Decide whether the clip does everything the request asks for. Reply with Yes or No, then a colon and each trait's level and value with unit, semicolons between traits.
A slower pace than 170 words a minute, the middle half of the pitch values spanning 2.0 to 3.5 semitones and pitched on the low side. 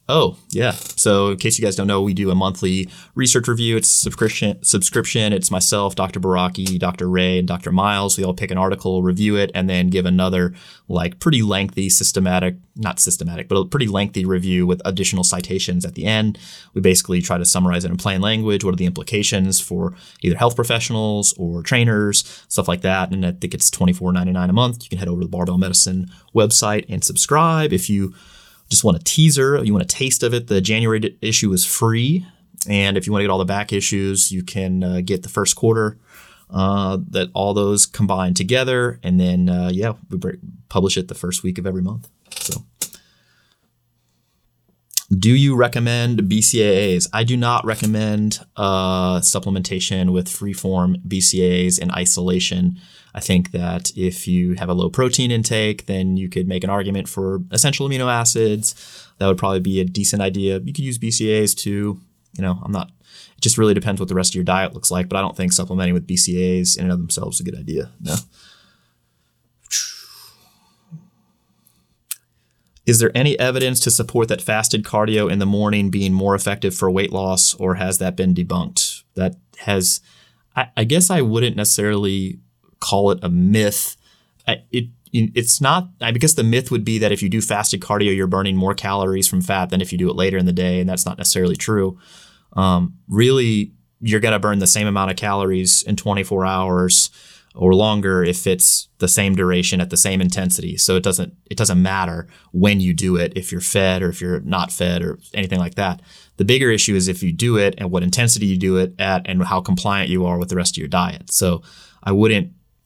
No: average, 200 wpm; average, 2.9 semitones; very low, 95 Hz